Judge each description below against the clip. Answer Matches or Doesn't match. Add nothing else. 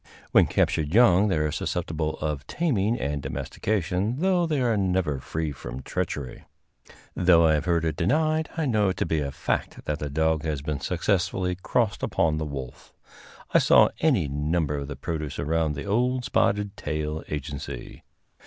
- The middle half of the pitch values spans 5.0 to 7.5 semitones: Matches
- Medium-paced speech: Matches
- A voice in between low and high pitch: Doesn't match